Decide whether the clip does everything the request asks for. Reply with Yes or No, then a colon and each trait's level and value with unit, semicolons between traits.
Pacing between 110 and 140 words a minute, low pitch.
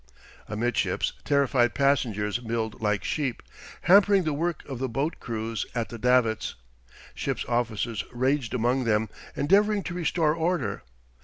Yes: slow, 135 wpm; low, 125 Hz